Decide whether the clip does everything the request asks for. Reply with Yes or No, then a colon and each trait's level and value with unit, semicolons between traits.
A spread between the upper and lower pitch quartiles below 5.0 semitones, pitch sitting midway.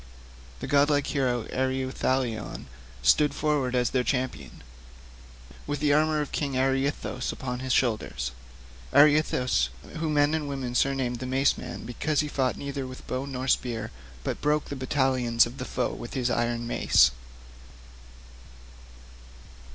No: average, 2.8 semitones; low, 130 Hz